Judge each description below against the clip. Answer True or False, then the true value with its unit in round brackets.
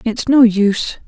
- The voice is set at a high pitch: True (225 Hz)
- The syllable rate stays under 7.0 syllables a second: True (4.4 syllables/s)